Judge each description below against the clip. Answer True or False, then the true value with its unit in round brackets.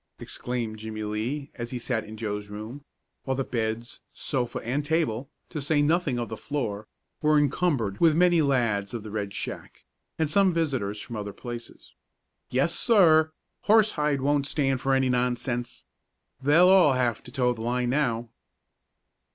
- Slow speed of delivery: False (160 wpm)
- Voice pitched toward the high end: False (125 Hz)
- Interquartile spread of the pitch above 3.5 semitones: True (4.7 semitones)